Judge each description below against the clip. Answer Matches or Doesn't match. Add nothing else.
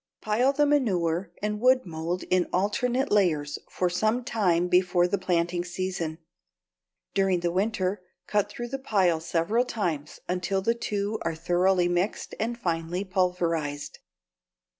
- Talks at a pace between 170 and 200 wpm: Doesn't match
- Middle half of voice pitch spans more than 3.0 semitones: Matches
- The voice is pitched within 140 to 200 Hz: Matches